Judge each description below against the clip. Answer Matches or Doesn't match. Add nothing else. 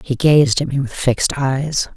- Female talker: Matches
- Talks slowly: Doesn't match